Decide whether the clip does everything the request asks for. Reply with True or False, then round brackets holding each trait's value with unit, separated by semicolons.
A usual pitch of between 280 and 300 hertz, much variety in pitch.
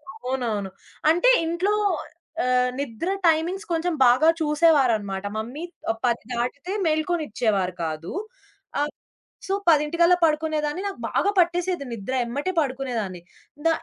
True (295 Hz; 6.2 semitones)